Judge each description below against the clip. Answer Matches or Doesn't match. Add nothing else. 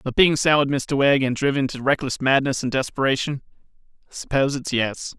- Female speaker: Doesn't match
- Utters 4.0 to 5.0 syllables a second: Doesn't match